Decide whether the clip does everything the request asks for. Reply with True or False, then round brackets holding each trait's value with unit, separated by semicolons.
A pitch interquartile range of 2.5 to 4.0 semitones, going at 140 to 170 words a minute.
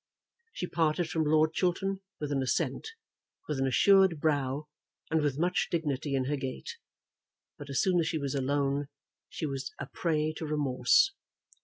True (3.0 semitones; 165 wpm)